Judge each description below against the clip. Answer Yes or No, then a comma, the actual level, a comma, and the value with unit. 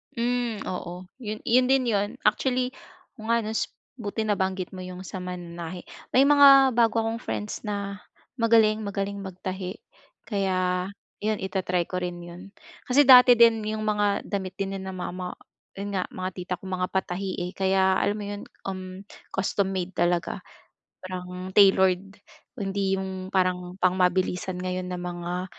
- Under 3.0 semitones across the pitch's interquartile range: Yes, narrow, 2.6 semitones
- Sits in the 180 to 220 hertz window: Yes, high, 190 Hz